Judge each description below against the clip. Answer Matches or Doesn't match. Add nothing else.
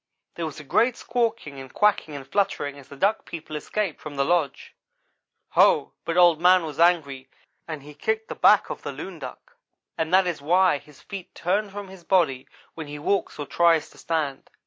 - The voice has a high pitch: Doesn't match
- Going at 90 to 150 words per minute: Doesn't match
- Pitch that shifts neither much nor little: Matches